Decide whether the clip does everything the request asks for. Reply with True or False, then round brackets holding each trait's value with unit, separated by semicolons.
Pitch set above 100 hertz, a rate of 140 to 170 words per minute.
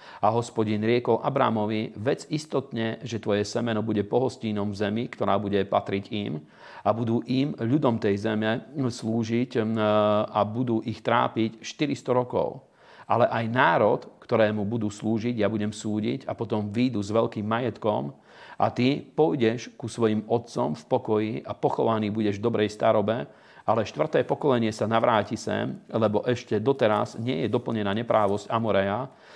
True (110 Hz; 150 wpm)